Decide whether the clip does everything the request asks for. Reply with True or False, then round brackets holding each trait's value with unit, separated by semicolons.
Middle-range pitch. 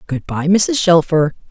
True (170 Hz)